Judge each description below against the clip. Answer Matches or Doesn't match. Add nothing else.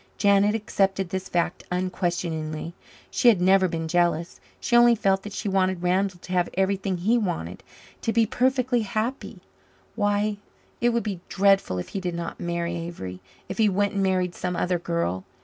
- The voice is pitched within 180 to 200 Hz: Matches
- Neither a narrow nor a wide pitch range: Matches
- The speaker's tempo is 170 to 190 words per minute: Matches